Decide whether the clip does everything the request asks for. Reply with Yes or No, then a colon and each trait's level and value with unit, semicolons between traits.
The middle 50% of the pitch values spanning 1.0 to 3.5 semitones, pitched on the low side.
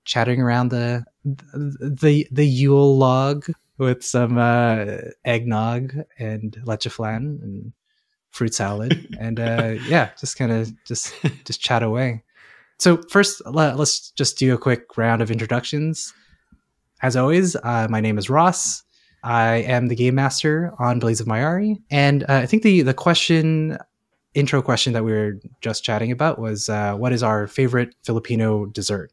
No: average, 4.3 semitones; low, 125 Hz